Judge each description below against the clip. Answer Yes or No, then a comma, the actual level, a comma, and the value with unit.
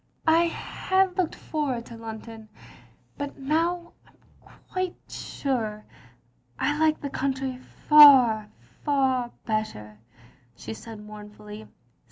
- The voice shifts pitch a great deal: Yes, wide, 5.9 semitones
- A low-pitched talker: No, very high, 260 Hz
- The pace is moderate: No, slow, 120 wpm